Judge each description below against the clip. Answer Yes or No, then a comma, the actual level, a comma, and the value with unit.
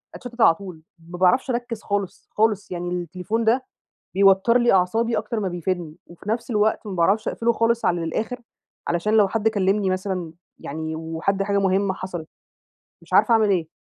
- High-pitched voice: Yes, high, 195 Hz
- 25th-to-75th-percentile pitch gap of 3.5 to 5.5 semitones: Yes, average, 3.9 semitones